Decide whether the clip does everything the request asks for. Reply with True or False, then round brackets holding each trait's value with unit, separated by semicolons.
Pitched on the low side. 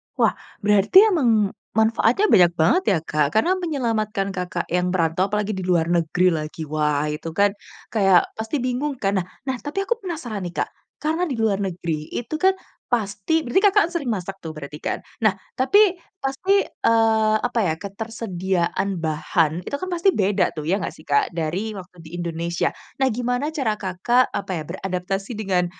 False (200 Hz)